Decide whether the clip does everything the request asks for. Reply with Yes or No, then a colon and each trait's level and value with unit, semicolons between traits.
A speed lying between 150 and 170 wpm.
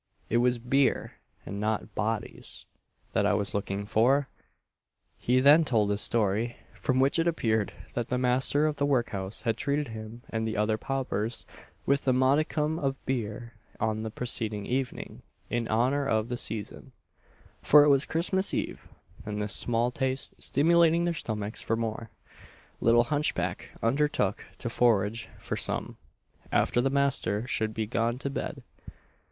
Yes: average, 155 wpm